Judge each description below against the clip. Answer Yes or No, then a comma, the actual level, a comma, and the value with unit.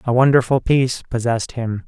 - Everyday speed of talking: Yes, average, 160 wpm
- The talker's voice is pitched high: No, low, 125 Hz